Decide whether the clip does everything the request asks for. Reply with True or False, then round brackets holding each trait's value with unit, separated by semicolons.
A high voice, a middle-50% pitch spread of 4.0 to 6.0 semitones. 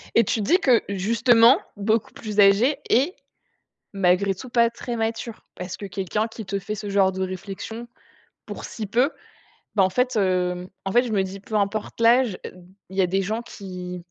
False (205 Hz; 3.4 semitones)